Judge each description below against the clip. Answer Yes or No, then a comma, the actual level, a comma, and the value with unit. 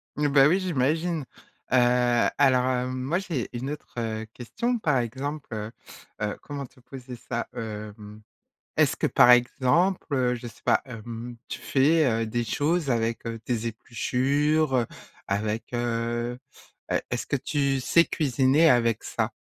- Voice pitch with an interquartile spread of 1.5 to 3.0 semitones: No, average, 3.7 semitones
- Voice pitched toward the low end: Yes, low, 125 Hz